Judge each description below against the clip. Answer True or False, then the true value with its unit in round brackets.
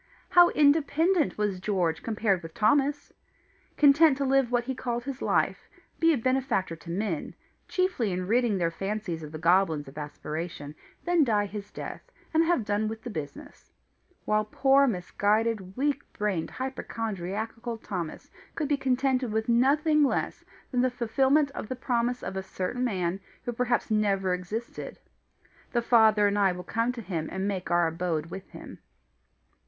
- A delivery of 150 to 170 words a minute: True (165 wpm)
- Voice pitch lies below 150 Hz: False (220 Hz)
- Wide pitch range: True (5.9 semitones)